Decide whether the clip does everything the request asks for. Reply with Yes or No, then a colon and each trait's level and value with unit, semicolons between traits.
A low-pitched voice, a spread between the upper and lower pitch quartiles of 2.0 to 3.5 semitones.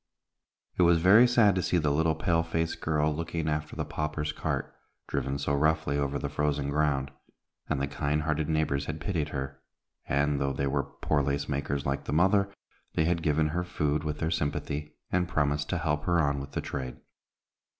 Yes: very low, 75 Hz; narrow, 2.4 semitones